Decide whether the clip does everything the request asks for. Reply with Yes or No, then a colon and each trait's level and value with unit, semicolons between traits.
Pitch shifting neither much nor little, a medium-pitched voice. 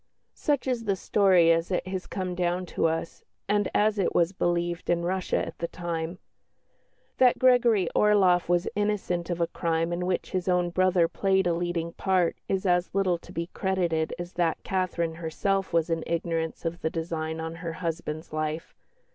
No: narrow, 2.2 semitones; medium, 175 Hz